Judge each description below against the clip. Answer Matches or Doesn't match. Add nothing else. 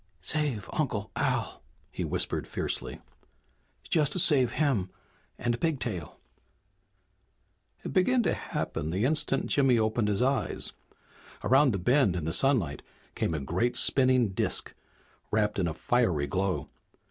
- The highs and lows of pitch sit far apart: Matches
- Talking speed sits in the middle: Doesn't match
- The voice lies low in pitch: Matches